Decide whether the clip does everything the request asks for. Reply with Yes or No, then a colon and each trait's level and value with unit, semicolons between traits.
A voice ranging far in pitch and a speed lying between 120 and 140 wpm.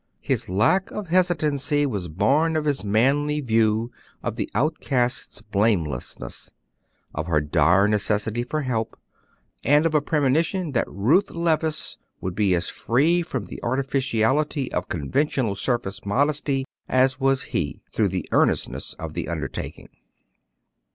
Yes: wide, 6.2 semitones; slow, 135 wpm